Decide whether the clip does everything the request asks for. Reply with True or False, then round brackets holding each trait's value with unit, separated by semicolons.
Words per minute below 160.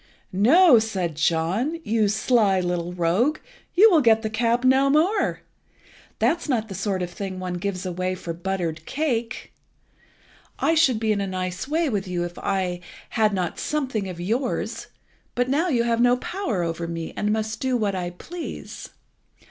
False (170 wpm)